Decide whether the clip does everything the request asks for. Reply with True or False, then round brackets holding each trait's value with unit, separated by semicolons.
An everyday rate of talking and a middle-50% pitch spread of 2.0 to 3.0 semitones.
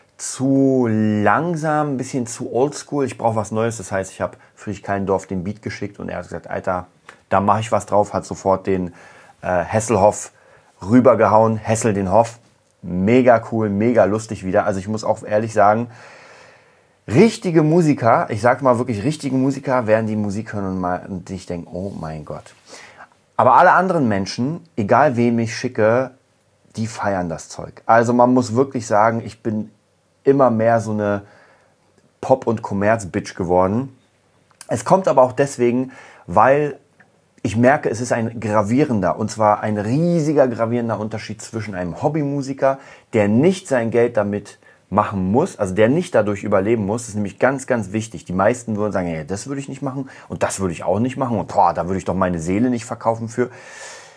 False (180 wpm; 3.7 semitones)